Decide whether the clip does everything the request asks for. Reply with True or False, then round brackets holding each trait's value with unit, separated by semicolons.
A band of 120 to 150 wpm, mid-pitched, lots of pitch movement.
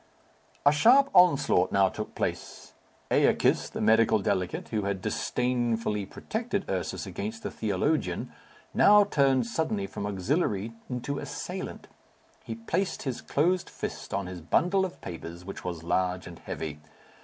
False (140 wpm; 115 Hz; 8.9 semitones)